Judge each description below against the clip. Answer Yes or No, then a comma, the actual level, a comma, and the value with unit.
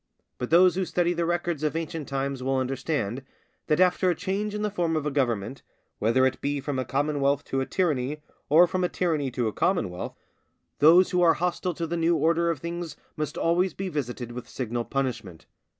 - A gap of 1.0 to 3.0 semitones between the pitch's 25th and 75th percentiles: No, average, 4.7 semitones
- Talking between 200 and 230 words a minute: Yes, fast, 205 wpm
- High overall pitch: No, medium, 150 Hz